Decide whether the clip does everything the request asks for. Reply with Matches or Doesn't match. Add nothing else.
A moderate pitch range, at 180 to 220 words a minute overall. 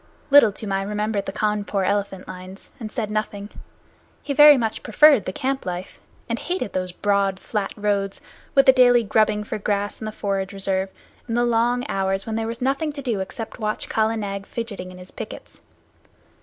Matches